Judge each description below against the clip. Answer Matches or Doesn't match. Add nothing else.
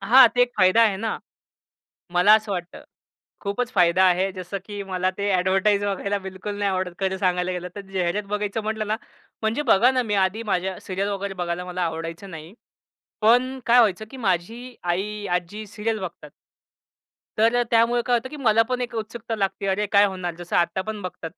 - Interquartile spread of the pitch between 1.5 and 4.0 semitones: Matches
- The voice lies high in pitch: Matches